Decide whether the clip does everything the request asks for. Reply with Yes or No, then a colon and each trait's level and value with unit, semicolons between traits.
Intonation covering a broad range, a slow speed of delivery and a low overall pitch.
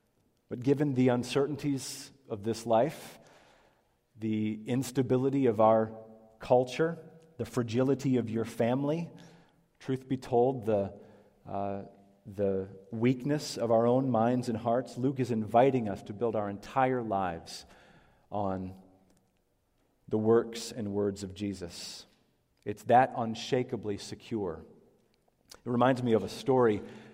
No: average, 3.7 semitones; slow, 125 wpm; low, 115 Hz